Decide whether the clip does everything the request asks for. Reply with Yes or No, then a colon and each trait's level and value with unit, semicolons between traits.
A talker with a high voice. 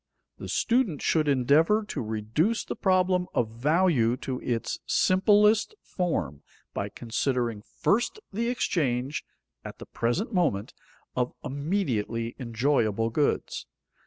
No: medium, 140 Hz